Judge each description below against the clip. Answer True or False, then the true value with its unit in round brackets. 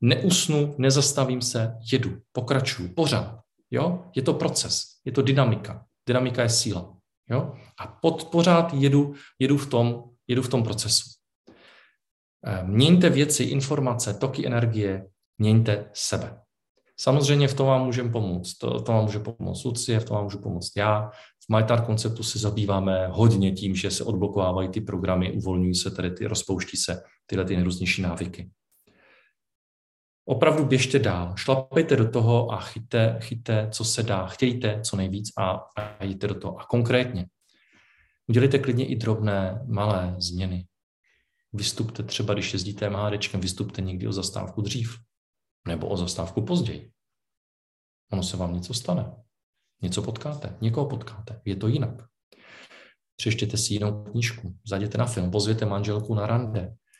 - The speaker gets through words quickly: False (145 wpm)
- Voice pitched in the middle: False (110 Hz)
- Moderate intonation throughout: True (4.6 semitones)